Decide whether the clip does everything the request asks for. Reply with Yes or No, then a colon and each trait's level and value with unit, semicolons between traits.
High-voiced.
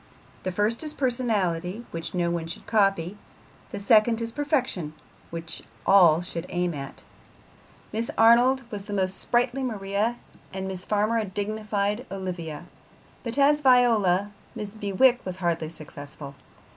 Yes: high, 200 Hz